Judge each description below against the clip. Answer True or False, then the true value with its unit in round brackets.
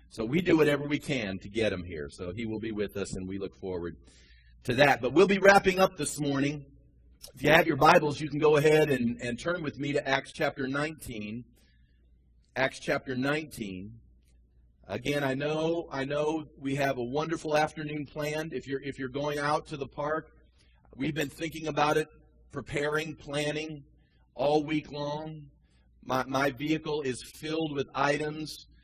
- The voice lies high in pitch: False (140 Hz)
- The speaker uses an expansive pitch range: True (5.9 semitones)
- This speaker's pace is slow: False (180 wpm)